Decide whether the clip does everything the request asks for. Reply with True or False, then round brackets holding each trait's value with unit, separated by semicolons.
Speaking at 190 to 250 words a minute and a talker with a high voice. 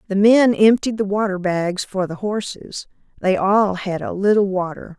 False (180 wpm; 200 Hz)